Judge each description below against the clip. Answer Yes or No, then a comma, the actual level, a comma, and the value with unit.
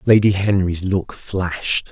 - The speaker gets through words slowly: Yes, slow, 125 wpm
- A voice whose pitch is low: Yes, very low, 95 Hz